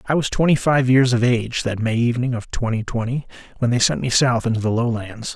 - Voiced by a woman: No, male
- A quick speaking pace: Yes, fast, 235 wpm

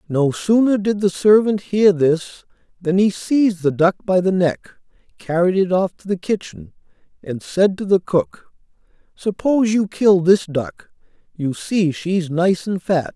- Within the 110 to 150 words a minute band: No, average, 170 wpm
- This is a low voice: No, medium, 185 Hz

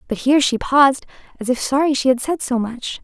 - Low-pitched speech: No, very high, 260 Hz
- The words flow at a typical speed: No, fast, 235 wpm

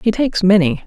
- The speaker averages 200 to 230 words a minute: Yes, fast, 205 wpm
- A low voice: No, high, 200 Hz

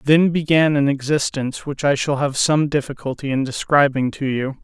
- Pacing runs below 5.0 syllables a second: No, 5.1 syllables/s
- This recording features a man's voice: Yes, male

